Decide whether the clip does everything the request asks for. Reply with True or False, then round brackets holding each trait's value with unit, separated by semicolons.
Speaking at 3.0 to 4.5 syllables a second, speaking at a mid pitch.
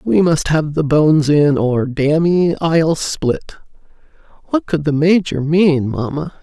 True (3.8 syllables/s; 155 Hz)